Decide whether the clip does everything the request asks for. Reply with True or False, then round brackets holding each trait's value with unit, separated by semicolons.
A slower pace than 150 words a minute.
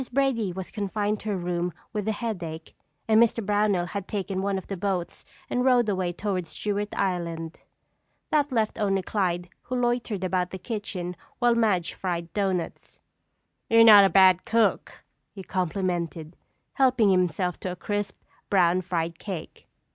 False (155 wpm)